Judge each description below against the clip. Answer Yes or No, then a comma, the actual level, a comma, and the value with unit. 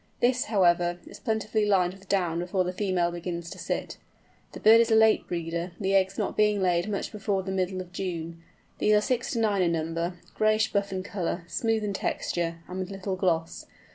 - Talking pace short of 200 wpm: No, fast, 205 wpm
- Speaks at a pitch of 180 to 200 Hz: Yes, high, 190 Hz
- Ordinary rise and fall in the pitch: Yes, average, 3.3 semitones